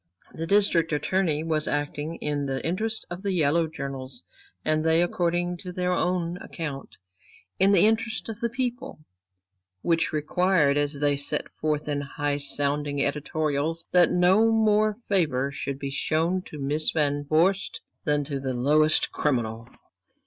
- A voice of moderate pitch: Yes, medium, 155 Hz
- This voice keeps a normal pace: Yes, average, 150 wpm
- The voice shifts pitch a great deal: No, average, 3.9 semitones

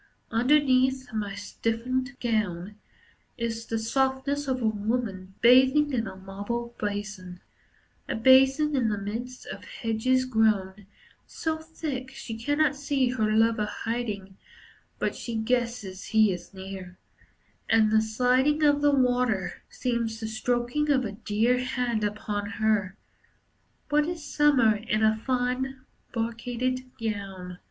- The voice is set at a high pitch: Yes, high, 230 Hz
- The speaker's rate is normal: No, slow, 130 wpm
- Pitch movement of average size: Yes, average, 3.5 semitones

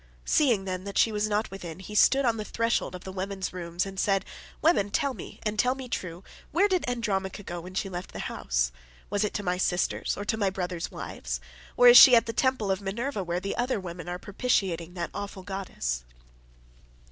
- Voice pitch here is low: No, high, 195 Hz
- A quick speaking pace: Yes, fast, 215 wpm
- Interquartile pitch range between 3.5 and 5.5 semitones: Yes, average, 4.0 semitones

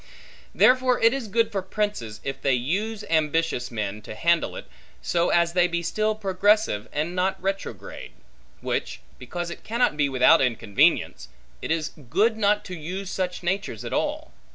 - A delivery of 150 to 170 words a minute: Yes, average, 165 wpm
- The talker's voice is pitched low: No, medium, 180 Hz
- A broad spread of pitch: Yes, wide, 5.8 semitones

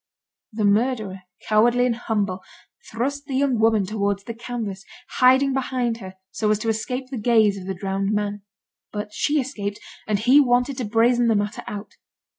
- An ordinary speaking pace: Yes, average, 175 wpm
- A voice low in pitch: No, high, 225 Hz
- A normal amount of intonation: Yes, average, 3.4 semitones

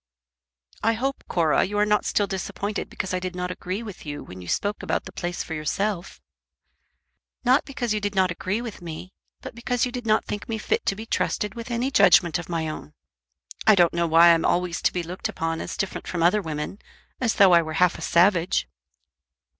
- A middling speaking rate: No, fast, 215 wpm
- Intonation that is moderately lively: Yes, average, 4.0 semitones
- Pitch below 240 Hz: Yes, medium, 185 Hz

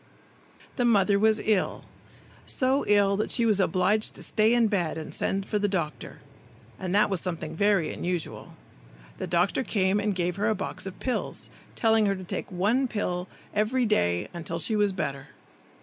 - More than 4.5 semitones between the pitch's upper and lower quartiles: No, average, 3.2 semitones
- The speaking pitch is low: No, high, 200 Hz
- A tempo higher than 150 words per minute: Yes, average, 175 wpm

